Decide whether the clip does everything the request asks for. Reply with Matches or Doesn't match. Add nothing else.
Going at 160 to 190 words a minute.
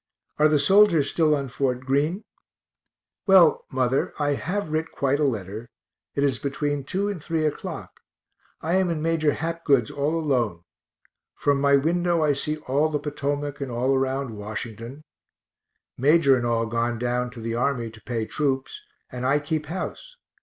Matches